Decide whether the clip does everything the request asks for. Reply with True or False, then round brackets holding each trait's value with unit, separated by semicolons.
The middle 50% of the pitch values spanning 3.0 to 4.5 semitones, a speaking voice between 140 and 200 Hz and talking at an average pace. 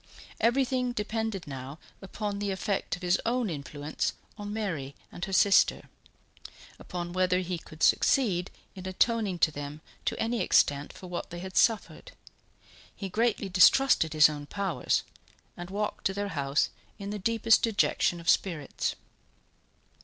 True (4.1 semitones; 190 Hz; 145 wpm)